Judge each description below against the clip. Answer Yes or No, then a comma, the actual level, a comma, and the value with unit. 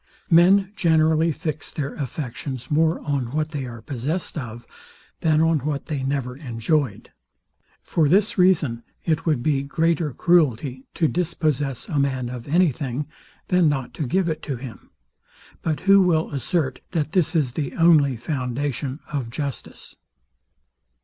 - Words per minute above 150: No, average, 145 wpm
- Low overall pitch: No, medium, 150 Hz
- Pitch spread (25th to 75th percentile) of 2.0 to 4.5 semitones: Yes, average, 3.7 semitones